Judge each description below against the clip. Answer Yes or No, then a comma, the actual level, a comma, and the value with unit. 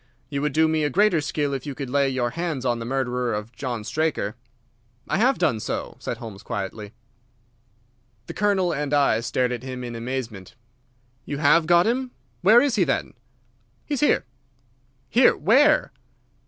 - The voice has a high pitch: No, medium, 140 Hz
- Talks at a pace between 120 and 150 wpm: No, average, 175 wpm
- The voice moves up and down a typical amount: No, wide, 6.1 semitones